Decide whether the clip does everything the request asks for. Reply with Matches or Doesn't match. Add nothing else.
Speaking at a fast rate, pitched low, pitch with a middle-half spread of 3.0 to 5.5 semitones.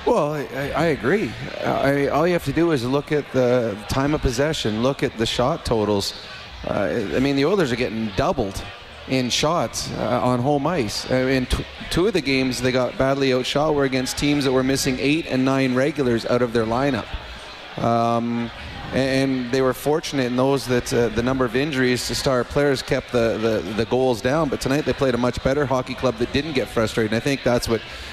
Doesn't match